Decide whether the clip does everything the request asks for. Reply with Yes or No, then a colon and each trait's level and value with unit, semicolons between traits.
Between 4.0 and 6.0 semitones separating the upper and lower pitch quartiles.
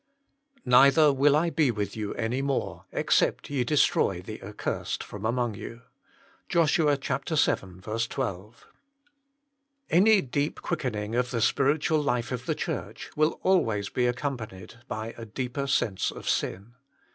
Yes: average, 4.4 semitones